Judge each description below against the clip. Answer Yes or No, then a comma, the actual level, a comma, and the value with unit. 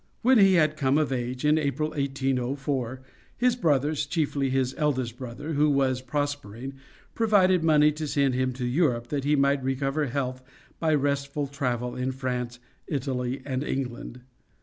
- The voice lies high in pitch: No, medium, 140 Hz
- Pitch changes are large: No, average, 2.7 semitones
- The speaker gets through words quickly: No, average, 155 wpm